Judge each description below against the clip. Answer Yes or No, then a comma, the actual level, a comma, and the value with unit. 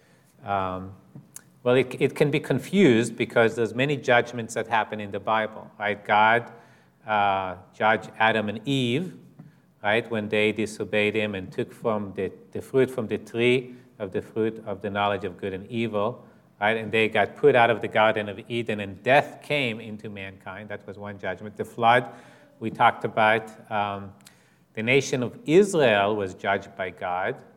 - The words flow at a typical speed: Yes, average, 175 wpm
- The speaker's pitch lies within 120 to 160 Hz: No, low, 110 Hz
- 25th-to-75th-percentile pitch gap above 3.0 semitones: No, narrow, 2.5 semitones